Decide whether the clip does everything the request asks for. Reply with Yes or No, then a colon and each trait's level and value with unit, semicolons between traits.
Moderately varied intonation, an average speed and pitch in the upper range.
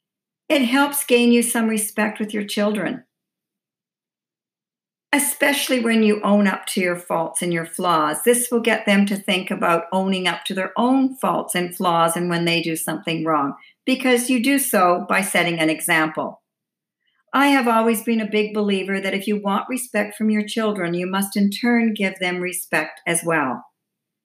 Yes: average, 4.8 semitones; average, 180 wpm; high, 205 Hz